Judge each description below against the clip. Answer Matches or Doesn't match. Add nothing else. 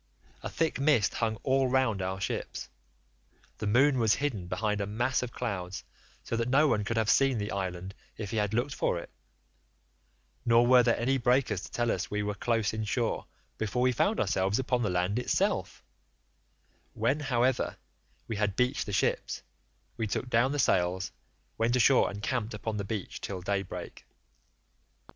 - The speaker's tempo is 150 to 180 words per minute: Matches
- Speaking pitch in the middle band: Doesn't match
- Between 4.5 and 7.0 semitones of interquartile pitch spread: Doesn't match